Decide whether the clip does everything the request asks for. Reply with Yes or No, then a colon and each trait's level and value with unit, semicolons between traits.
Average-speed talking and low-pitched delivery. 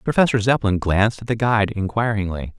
Yes: average, 160 wpm; low, 105 Hz